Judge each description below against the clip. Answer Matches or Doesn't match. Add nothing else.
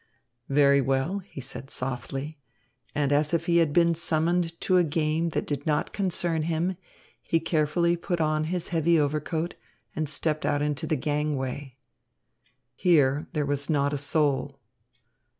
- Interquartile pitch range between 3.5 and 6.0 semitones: Doesn't match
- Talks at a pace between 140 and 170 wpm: Matches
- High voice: Doesn't match